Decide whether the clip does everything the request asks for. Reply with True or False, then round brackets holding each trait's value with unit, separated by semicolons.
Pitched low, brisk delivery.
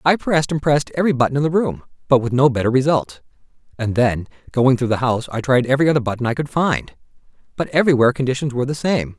True (130 Hz; 220 wpm)